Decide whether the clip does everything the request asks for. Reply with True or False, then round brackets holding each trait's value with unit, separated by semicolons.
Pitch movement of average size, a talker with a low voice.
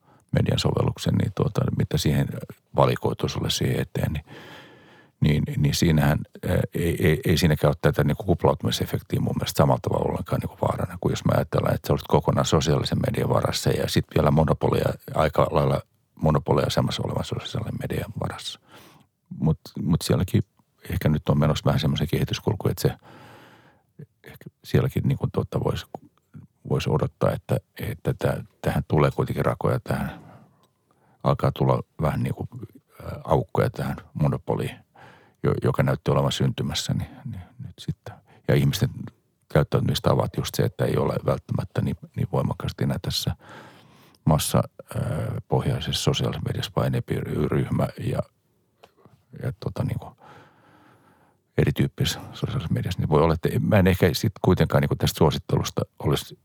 False (7.4 semitones; 80 Hz)